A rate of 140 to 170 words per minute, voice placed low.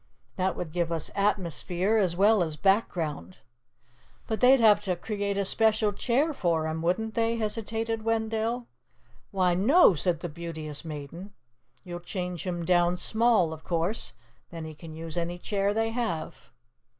No: average, 160 wpm; medium, 185 Hz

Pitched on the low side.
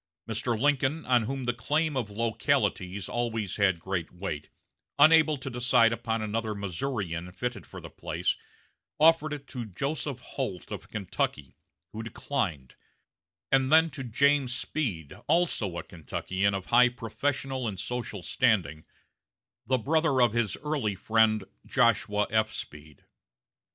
Yes: low, 115 Hz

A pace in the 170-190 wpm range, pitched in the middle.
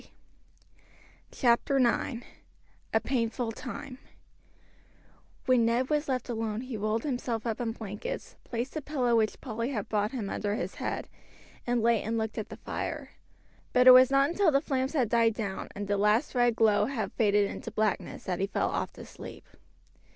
No: average, 180 wpm; high, 235 Hz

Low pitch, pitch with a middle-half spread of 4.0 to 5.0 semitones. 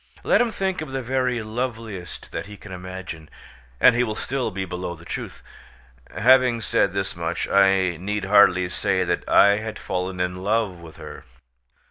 Yes: low, 100 Hz; average, 4.3 semitones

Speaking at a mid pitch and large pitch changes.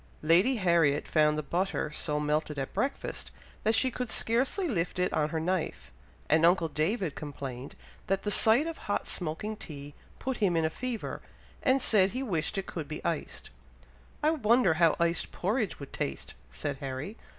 Yes: medium, 175 Hz; wide, 6.4 semitones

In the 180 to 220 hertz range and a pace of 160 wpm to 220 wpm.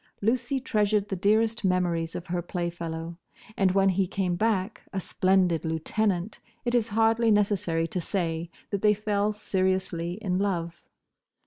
No: high, 190 Hz; average, 145 wpm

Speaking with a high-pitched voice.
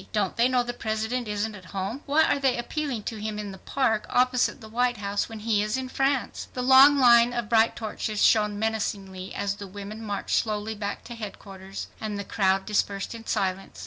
Yes: high, 220 Hz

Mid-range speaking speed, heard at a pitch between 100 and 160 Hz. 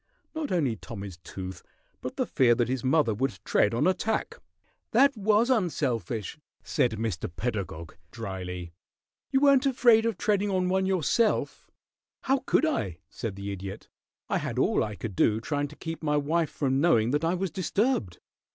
Yes: average, 170 wpm; medium, 140 Hz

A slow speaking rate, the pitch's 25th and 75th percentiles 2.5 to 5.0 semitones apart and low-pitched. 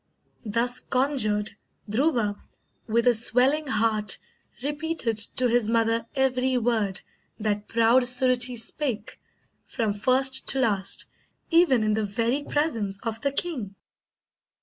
No: slow, 120 wpm; average, 3.4 semitones; high, 235 Hz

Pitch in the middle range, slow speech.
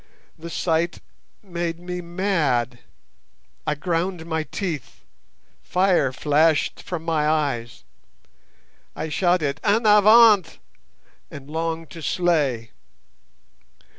Yes: medium, 165 Hz; slow, 95 wpm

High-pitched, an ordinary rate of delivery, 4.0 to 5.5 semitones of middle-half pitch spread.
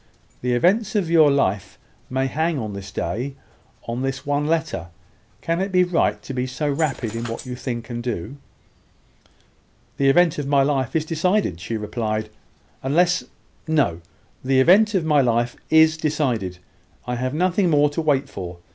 No: medium, 140 Hz; average, 170 wpm; average, 5.0 semitones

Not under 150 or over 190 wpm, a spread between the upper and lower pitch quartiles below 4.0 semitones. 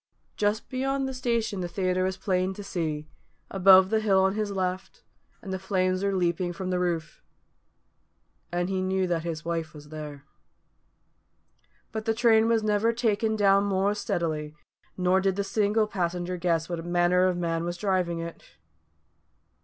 Yes: average, 165 wpm; average, 2.9 semitones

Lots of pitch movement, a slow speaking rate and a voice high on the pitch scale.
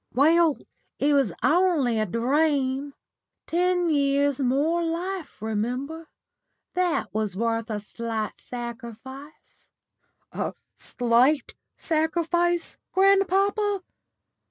Yes: wide, 6.2 semitones; slow, 85 wpm; very high, 285 Hz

